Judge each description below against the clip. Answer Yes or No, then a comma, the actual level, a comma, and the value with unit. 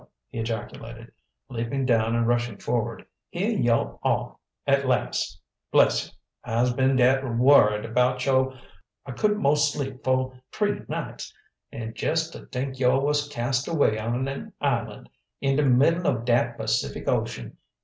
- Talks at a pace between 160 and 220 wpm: No, average, 150 wpm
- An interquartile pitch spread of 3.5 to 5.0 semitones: No, average, 2.8 semitones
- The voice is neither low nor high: No, low, 130 Hz